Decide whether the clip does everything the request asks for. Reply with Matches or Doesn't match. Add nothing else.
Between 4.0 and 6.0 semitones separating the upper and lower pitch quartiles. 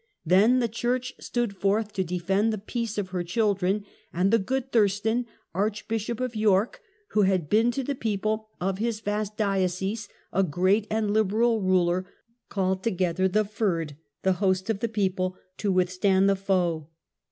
Doesn't match